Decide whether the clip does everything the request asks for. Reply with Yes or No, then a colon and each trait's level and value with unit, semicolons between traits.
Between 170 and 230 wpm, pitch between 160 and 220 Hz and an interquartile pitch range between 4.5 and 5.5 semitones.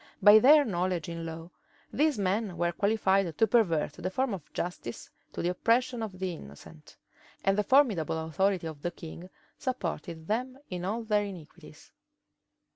No: average, 160 wpm; medium, 185 Hz; average, 4.8 semitones